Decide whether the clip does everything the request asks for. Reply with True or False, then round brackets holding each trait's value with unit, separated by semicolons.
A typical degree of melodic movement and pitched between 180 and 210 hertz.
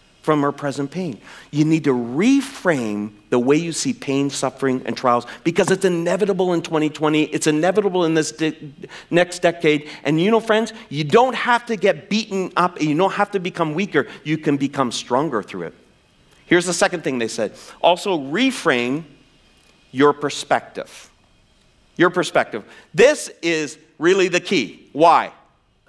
False (4.9 semitones; 160 Hz)